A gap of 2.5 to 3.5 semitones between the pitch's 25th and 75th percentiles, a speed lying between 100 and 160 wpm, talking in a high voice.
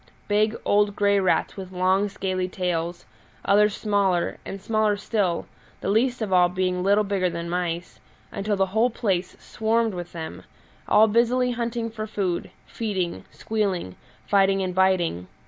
Yes: average, 3.0 semitones; average, 150 wpm; high, 195 Hz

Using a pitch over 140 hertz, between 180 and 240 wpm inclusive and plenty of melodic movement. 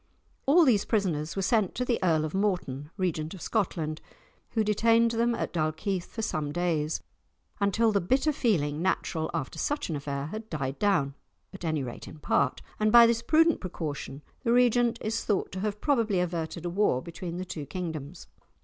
Yes: medium, 185 Hz; average, 185 wpm; wide, 6.3 semitones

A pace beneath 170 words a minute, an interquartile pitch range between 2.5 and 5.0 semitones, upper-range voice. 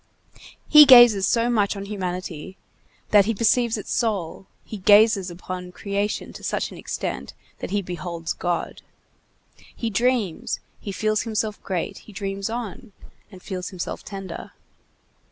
Yes: average, 140 wpm; average, 3.2 semitones; high, 200 Hz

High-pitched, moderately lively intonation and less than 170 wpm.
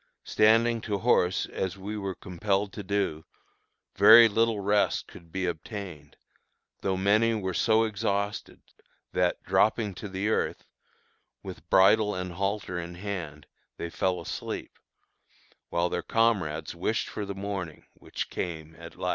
No: low, 100 Hz; average, 3.1 semitones; average, 140 wpm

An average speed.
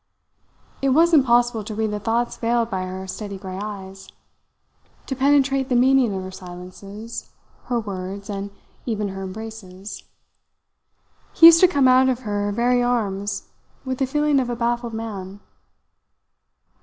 Yes: average, 150 wpm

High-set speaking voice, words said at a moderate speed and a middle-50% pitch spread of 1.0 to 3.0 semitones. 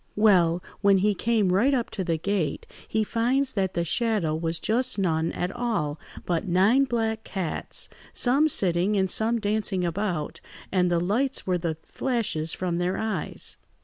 No: high, 195 Hz; average, 165 wpm; average, 4.6 semitones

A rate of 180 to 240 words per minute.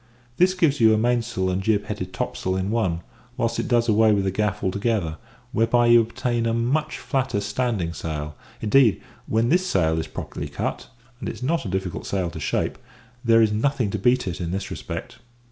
Yes: average, 200 wpm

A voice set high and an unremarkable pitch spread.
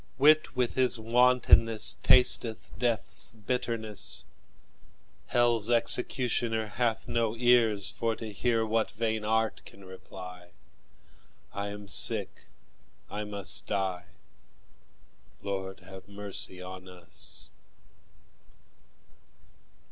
No: low, 110 Hz; average, 3.3 semitones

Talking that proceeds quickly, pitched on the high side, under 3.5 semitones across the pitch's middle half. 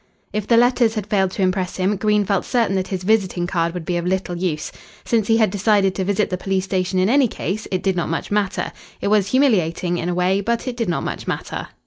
Yes: fast, 250 wpm; high, 195 Hz; average, 2.7 semitones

